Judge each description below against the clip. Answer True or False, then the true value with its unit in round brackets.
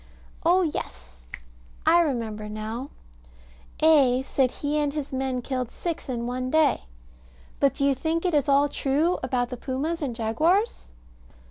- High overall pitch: True (270 Hz)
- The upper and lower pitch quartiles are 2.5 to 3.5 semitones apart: False (3.9 semitones)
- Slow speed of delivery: False (150 wpm)